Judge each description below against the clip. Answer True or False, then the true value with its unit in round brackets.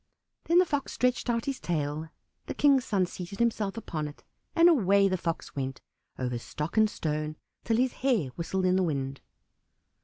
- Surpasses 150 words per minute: True (180 wpm)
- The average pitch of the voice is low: False (185 Hz)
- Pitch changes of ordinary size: False (7.6 semitones)